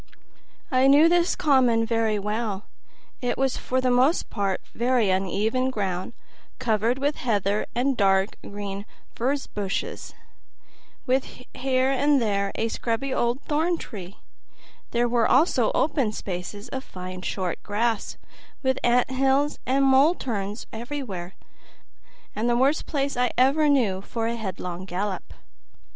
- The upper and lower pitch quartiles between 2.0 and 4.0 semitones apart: No, average, 4.7 semitones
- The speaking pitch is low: No, high, 240 Hz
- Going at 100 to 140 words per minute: Yes, slow, 135 wpm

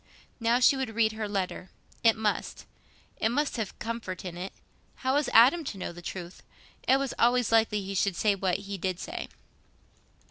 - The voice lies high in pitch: Yes, high, 220 Hz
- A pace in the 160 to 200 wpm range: Yes, average, 180 wpm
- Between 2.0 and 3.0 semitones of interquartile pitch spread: No, average, 3.8 semitones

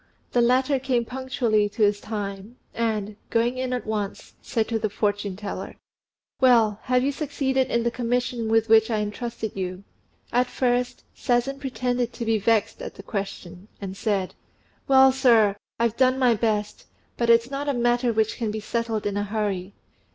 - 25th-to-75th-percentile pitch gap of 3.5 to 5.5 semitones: No, average, 3.1 semitones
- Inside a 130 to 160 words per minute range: No, average, 175 wpm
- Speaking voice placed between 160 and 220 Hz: No, high, 230 Hz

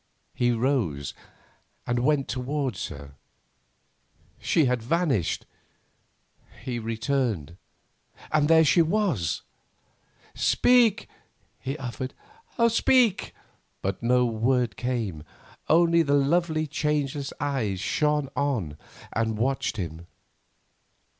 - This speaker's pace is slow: Yes, slow, 95 wpm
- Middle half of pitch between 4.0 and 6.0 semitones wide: Yes, average, 5.1 semitones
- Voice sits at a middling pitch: No, low, 130 Hz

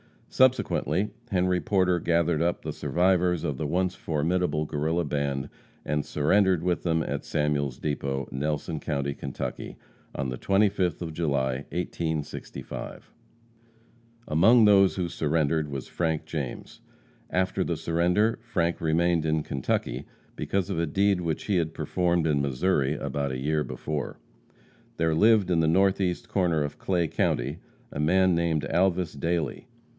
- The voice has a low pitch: Yes, very low, 80 Hz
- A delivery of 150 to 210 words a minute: No, average, 140 wpm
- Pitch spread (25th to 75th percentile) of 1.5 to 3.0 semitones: No, average, 3.5 semitones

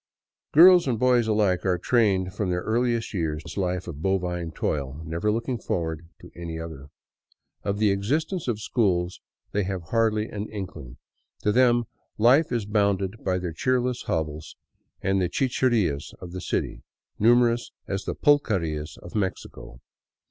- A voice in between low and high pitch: No, low, 100 Hz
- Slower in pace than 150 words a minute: No, average, 155 wpm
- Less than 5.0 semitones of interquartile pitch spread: No, average, 5.3 semitones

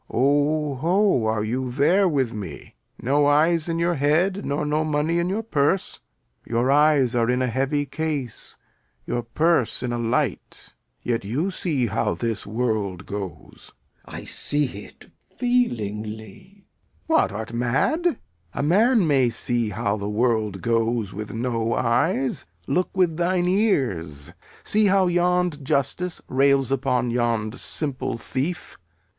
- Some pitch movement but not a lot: No, wide, 6.4 semitones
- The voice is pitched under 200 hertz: Yes, low, 135 Hz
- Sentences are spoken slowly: No, average, 145 wpm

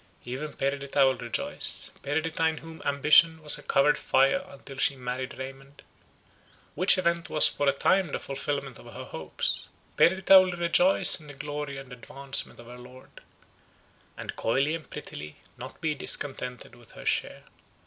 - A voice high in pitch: No, medium, 140 Hz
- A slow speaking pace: No, average, 160 wpm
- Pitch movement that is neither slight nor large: Yes, average, 3.5 semitones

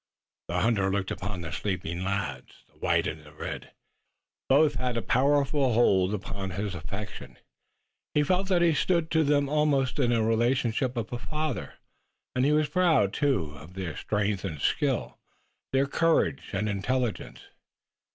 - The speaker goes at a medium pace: Yes, average, 160 wpm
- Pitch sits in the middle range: No, low, 120 Hz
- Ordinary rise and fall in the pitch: No, wide, 6.7 semitones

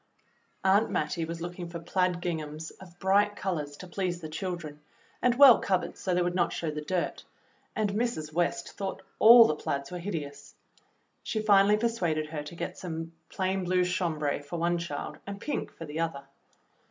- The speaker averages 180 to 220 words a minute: Yes, average, 185 wpm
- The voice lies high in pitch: No, medium, 175 Hz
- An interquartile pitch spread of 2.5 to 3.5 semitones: Yes, average, 3.2 semitones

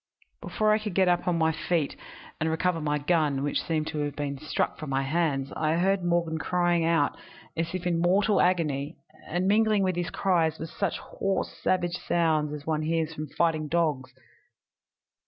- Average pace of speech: Yes, average, 180 wpm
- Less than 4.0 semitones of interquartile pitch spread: Yes, average, 2.7 semitones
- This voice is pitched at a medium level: Yes, medium, 165 Hz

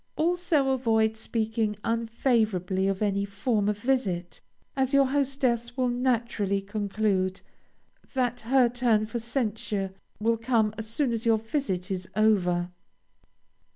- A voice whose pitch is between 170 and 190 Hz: No, high, 225 Hz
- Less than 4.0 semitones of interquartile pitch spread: Yes, average, 3.5 semitones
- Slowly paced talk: Yes, slow, 120 wpm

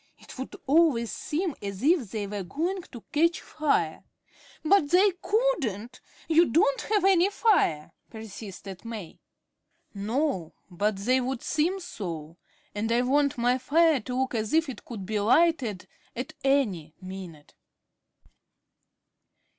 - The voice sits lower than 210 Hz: No, very high, 250 Hz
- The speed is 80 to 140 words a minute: Yes, slow, 135 wpm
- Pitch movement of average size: No, wide, 7.7 semitones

